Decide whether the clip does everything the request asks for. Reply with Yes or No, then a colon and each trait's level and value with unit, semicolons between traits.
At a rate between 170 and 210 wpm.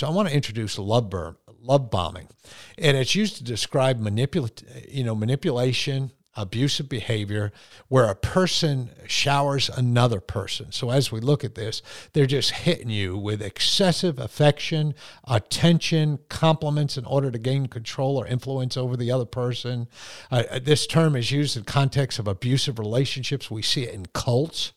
No: average, 160 wpm